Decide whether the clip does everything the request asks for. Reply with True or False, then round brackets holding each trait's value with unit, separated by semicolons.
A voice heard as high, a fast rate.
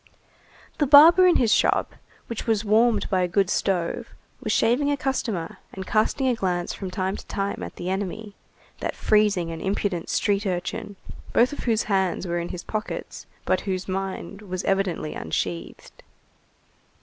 False (200 Hz; 165 wpm)